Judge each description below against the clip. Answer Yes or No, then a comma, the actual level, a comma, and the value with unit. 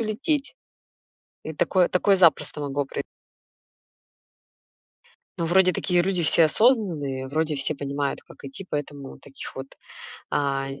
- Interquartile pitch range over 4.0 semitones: Yes, average, 4.9 semitones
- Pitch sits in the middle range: Yes, medium, 155 Hz